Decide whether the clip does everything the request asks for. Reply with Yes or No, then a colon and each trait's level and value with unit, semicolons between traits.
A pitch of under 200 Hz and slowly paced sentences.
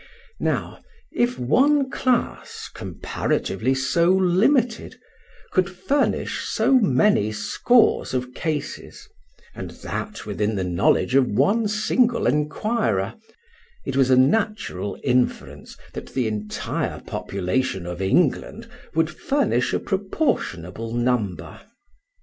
Yes: low, 135 Hz; slow, 105 wpm